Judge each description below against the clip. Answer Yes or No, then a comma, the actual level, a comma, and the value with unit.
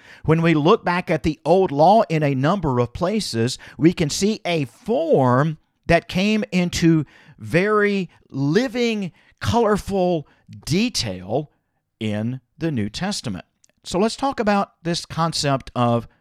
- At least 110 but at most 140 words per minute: Yes, slow, 135 wpm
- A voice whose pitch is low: No, medium, 165 Hz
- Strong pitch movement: Yes, wide, 7.0 semitones